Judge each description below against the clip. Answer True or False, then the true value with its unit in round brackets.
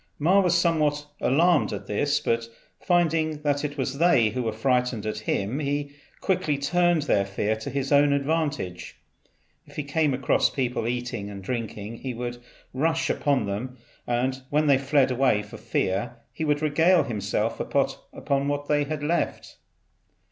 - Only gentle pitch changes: False (4.1 semitones)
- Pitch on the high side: False (140 Hz)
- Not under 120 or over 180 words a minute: True (160 wpm)